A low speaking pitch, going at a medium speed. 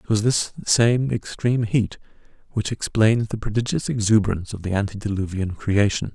Yes: low, 105 Hz; average, 145 wpm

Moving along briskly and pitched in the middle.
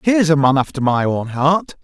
Yes: fast, 230 wpm; medium, 150 Hz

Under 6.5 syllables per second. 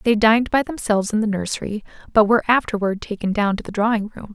No: 6.6 syllables/s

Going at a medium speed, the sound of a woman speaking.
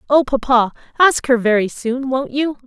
Yes: average, 180 wpm; female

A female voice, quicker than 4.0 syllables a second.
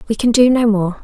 Yes: female; 5.9 syllables/s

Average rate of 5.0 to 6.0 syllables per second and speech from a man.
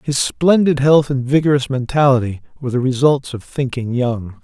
Yes: 5.1 syllables/s; male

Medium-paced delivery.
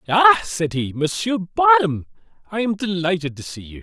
Yes: average, 175 wpm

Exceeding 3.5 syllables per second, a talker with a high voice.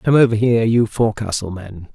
No: 6.0 syllables/s; low, 110 Hz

